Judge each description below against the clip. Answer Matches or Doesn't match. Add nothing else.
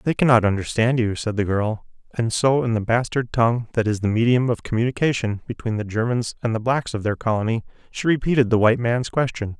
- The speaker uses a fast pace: Matches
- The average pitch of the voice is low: Matches